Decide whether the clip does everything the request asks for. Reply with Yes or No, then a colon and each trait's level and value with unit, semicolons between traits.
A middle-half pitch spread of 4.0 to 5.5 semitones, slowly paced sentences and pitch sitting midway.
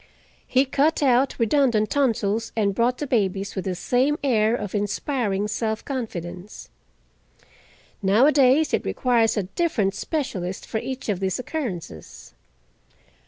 No: average, 4.9 semitones; slow, 125 wpm; high, 225 Hz